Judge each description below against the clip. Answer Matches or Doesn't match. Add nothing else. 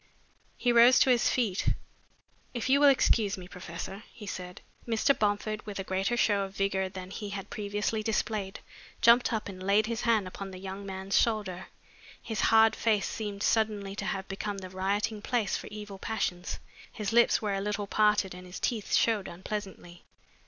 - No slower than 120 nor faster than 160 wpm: Doesn't match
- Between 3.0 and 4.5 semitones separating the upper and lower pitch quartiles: Doesn't match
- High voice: Matches